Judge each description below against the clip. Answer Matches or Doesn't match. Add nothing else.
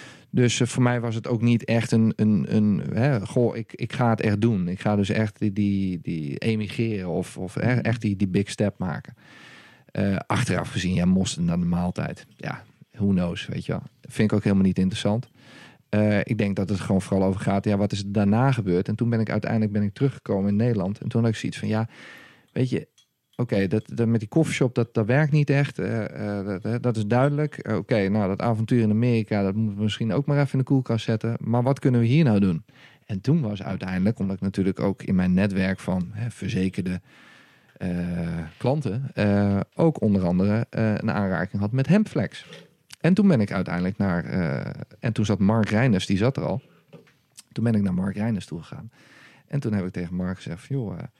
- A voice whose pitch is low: Matches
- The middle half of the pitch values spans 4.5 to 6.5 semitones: Doesn't match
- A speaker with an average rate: Doesn't match